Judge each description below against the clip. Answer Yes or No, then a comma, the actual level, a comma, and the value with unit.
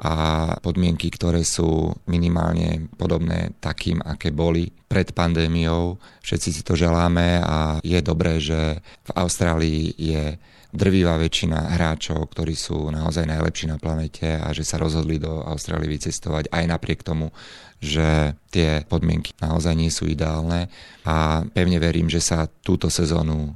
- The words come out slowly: No, average, 140 wpm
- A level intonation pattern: Yes, narrow, 1.5 semitones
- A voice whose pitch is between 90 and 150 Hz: No, very low, 80 Hz